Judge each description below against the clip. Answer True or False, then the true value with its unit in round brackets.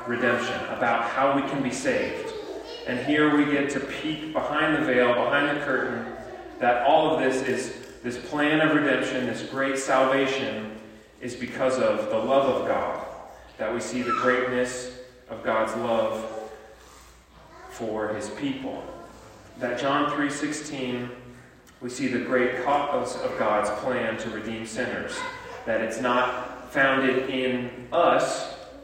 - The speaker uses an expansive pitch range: False (2.8 semitones)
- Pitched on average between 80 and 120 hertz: False (130 Hz)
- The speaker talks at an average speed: True (145 wpm)